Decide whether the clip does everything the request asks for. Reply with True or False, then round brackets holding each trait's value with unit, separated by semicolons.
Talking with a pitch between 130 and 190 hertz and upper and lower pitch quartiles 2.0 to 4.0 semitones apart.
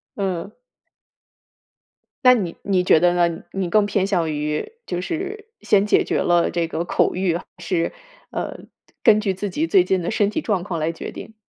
True (185 Hz; 3.6 semitones)